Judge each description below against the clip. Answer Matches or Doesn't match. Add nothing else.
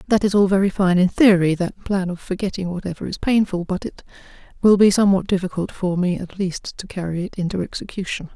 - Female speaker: Matches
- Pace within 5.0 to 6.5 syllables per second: Matches